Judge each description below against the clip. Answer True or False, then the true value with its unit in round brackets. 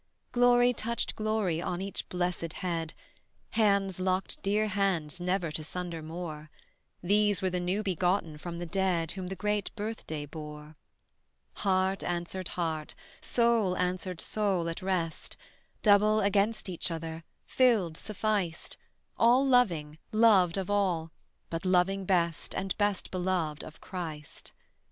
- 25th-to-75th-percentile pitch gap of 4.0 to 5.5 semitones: False (3.4 semitones)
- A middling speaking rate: False (130 wpm)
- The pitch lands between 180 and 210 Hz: True (185 Hz)